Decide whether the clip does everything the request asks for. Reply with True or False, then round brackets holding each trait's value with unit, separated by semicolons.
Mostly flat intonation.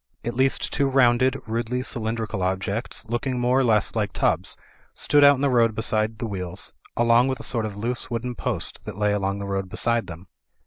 False (3.3 semitones)